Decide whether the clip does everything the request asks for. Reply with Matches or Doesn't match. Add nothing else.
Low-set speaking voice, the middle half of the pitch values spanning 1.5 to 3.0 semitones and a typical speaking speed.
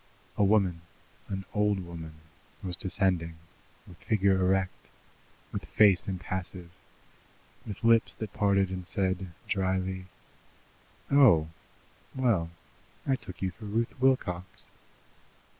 Doesn't match